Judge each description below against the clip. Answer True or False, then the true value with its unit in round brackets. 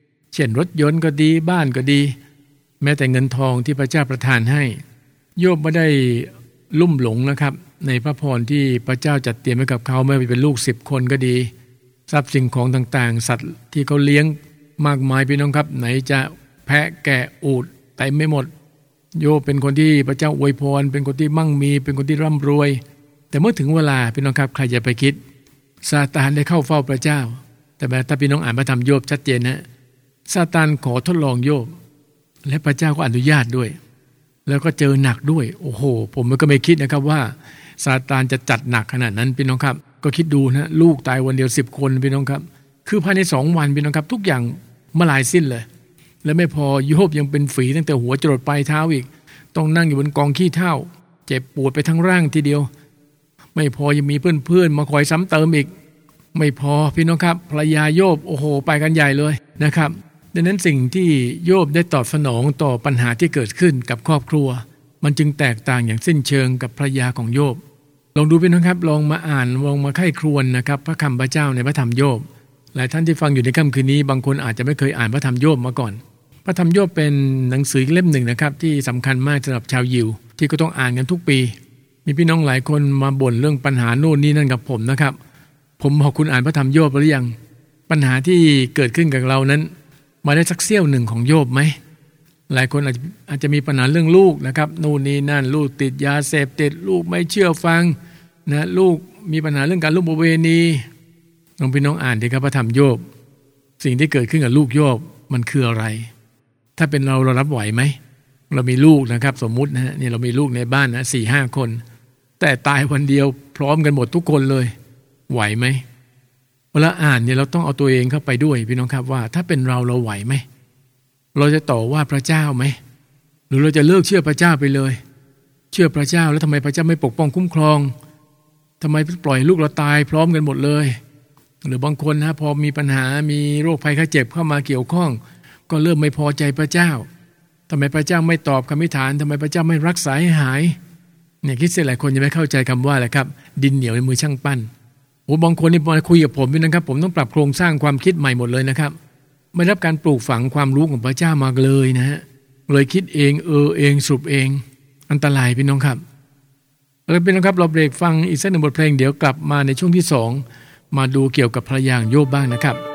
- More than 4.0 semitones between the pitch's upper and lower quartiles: False (2.6 semitones)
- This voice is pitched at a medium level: True (145 Hz)